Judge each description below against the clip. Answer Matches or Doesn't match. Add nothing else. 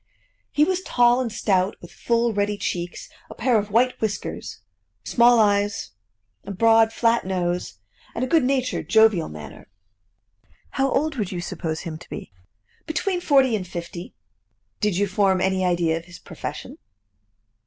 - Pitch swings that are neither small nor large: Matches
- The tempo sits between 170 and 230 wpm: Doesn't match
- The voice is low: Doesn't match